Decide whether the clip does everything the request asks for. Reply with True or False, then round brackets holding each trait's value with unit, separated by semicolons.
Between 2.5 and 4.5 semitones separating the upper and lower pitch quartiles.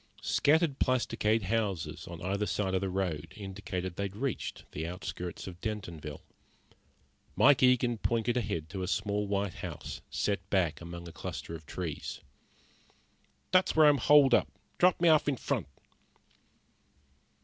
False (5.5 semitones)